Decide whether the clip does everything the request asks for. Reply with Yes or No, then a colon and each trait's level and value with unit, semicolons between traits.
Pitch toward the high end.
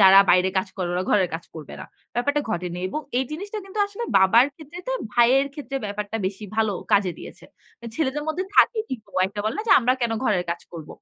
Yes: high, 225 Hz